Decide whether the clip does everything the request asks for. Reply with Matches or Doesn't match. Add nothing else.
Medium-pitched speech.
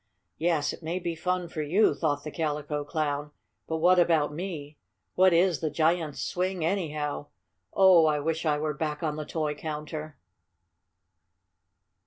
Matches